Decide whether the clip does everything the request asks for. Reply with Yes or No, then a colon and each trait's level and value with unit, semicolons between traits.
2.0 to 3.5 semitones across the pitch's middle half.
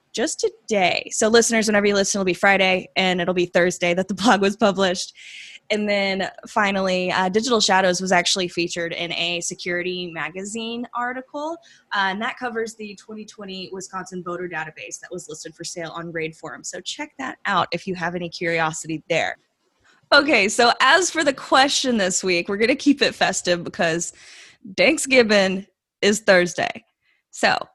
No: average, 4.5 semitones